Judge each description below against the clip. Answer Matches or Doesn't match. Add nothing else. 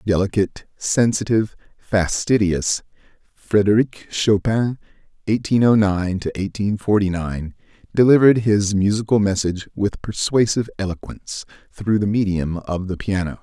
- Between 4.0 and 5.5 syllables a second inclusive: Matches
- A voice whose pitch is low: Matches